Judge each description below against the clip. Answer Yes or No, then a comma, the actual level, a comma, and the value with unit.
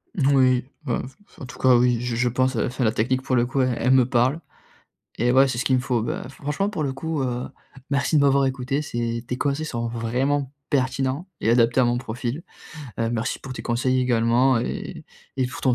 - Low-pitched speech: Yes, low, 130 Hz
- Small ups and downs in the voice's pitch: Yes, narrow, 2.0 semitones